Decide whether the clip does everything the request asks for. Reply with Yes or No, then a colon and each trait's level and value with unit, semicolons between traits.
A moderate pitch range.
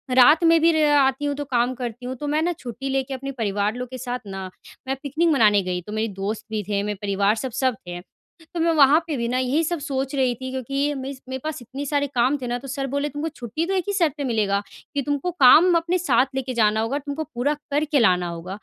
Yes: average, 4.1 semitones